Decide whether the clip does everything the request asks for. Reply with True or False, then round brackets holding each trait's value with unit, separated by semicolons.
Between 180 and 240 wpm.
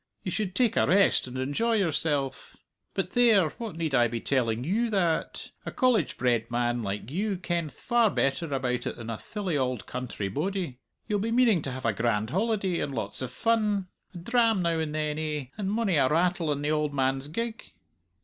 True (200 wpm)